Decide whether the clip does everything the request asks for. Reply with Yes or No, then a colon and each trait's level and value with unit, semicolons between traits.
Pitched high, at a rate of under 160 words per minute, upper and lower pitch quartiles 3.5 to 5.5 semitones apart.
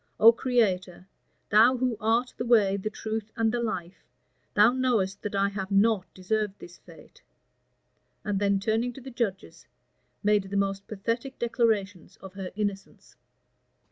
No: high, 210 Hz; average, 150 wpm; average, 2.9 semitones